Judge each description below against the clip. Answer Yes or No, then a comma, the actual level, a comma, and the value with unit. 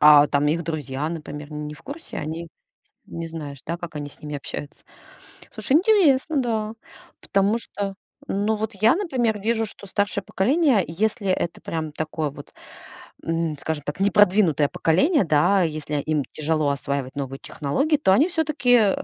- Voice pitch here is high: No, medium, 170 Hz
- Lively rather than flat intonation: Yes, wide, 6.6 semitones